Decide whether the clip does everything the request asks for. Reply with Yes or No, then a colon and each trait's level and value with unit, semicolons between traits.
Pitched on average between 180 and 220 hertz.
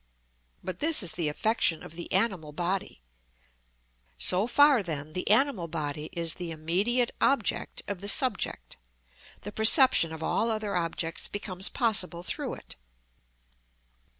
Yes: medium, 185 Hz